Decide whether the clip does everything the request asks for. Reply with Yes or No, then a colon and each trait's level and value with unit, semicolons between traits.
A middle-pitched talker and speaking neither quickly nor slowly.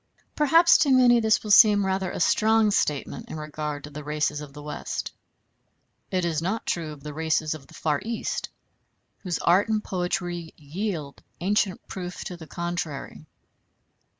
Yes: medium, 175 Hz; average, 165 wpm